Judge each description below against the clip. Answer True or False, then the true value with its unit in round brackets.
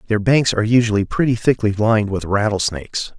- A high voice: False (110 Hz)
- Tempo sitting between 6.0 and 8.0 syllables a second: True (6.1 syllables/s)